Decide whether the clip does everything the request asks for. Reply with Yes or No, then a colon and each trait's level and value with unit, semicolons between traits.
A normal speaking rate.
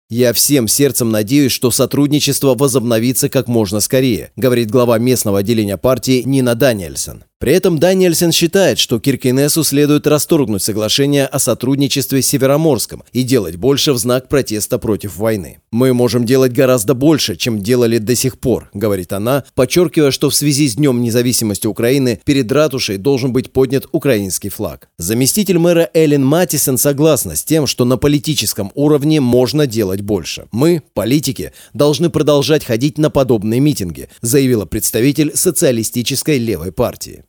Yes: average, 150 wpm